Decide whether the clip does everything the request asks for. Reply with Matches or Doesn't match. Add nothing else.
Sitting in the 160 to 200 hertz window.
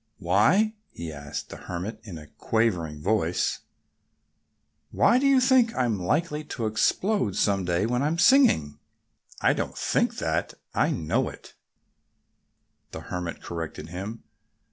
Doesn't match